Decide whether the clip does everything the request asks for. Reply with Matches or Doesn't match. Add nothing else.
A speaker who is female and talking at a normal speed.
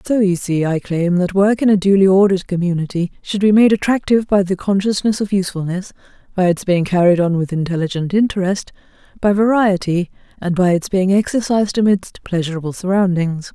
Matches